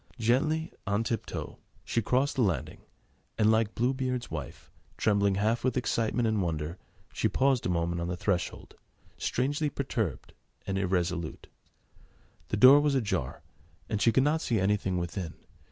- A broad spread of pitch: Yes, wide, 5.8 semitones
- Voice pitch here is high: No, low, 110 Hz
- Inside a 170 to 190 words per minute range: No, average, 155 wpm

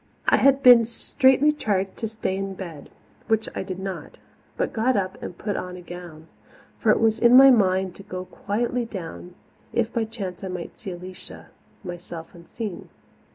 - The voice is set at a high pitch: Yes, high, 195 Hz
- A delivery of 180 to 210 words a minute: Yes, average, 185 wpm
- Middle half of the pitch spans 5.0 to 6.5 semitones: No, average, 4.1 semitones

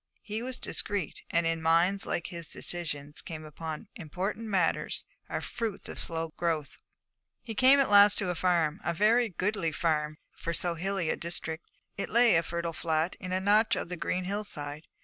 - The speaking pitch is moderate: Yes, medium, 175 Hz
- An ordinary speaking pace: Yes, average, 180 wpm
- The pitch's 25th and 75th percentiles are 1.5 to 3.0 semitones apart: No, average, 3.9 semitones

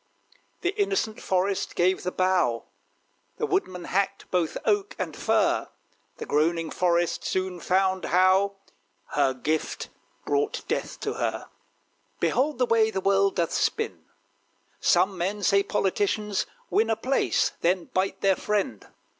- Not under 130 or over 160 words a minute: Yes, slow, 135 wpm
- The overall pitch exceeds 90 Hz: Yes, high, 190 Hz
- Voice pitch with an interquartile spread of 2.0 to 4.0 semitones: Yes, average, 2.8 semitones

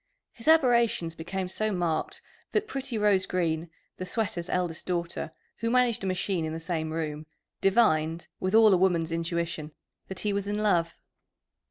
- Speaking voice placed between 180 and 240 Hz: Yes, medium, 185 Hz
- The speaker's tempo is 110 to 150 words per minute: No, average, 165 wpm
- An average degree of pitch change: Yes, average, 4.3 semitones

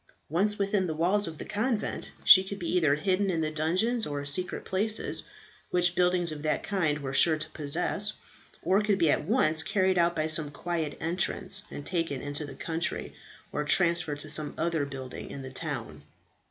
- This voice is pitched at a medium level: Yes, medium, 170 Hz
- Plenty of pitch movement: No, average, 3.9 semitones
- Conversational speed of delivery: Yes, average, 190 wpm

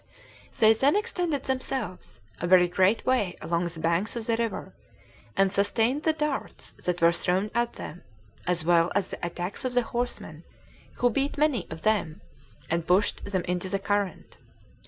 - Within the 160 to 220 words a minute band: Yes, average, 170 wpm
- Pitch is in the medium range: No, high, 200 Hz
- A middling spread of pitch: No, wide, 5.7 semitones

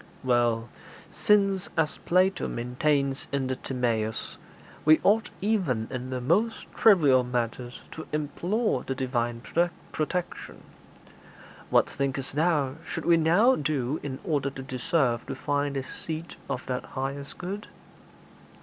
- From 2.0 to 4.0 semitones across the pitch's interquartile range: No, average, 5.0 semitones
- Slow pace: Yes, slow, 130 wpm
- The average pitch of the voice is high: No, medium, 140 Hz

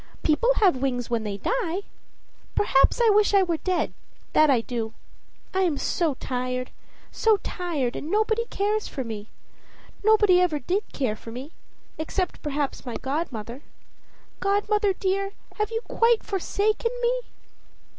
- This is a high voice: Yes, very high, 350 Hz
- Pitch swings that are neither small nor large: No, wide, 8.2 semitones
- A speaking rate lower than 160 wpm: Yes, average, 145 wpm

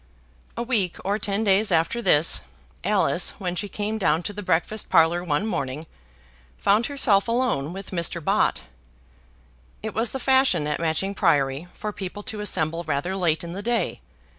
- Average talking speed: Yes, average, 165 wpm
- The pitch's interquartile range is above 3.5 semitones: Yes, average, 4.6 semitones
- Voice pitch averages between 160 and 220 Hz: Yes, high, 190 Hz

